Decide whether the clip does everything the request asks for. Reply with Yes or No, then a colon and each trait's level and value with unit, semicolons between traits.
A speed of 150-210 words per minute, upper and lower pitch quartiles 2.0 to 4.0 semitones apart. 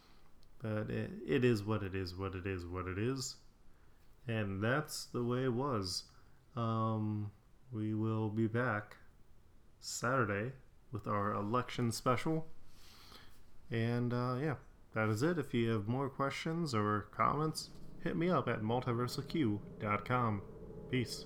No: slow, 135 wpm; average, 3.7 semitones